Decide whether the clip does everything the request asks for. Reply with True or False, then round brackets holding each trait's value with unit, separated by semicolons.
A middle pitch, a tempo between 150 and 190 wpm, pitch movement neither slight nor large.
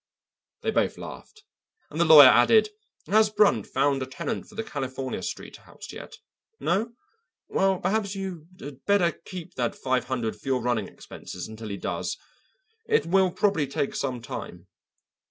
False (150 Hz; 160 wpm; 7.2 semitones)